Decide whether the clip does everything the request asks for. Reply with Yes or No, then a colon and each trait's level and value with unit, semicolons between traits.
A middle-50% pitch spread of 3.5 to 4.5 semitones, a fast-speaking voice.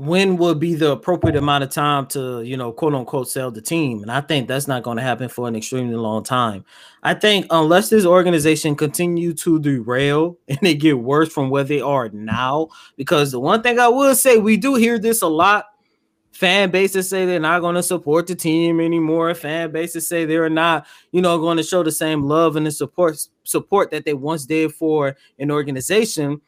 Yes: average, 4.0 semitones; fast, 215 wpm